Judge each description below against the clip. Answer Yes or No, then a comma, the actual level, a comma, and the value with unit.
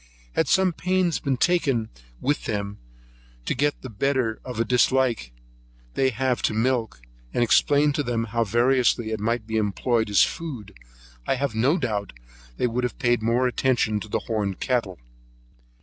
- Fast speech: No, average, 170 wpm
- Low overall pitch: Yes, low, 120 Hz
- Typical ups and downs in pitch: Yes, average, 3.4 semitones